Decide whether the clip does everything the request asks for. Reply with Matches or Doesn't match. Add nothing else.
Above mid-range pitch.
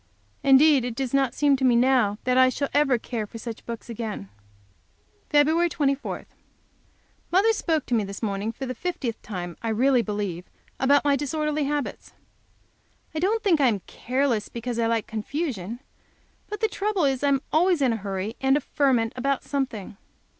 Matches